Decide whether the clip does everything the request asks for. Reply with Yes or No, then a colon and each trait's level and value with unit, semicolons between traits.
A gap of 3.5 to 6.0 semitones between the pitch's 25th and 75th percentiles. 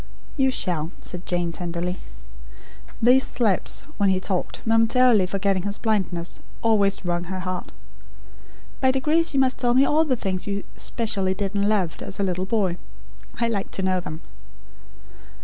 Yes: average, 4.1 semitones